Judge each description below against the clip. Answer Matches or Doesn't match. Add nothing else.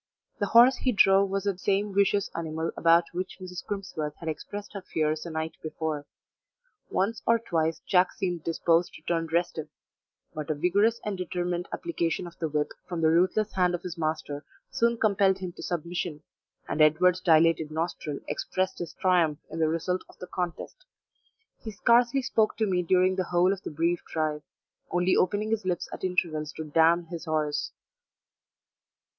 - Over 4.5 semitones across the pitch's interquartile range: Doesn't match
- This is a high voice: Doesn't match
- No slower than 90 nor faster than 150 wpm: Doesn't match